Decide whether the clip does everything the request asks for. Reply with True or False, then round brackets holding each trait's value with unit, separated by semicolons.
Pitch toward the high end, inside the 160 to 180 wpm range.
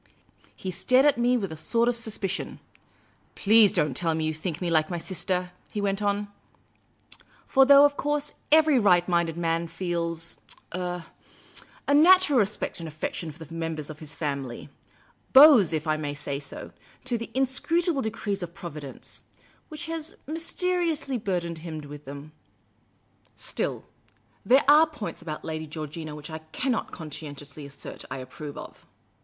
False (175 Hz; 175 wpm)